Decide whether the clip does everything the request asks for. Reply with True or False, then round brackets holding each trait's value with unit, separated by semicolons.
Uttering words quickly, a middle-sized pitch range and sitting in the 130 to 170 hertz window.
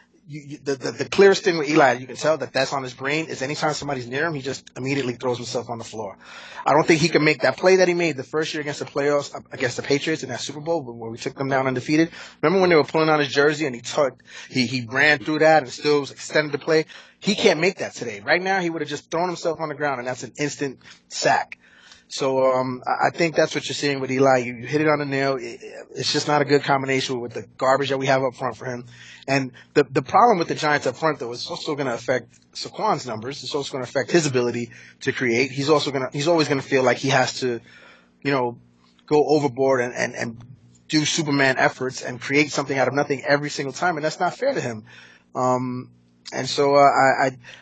True (255 wpm; 3.1 semitones; 140 Hz)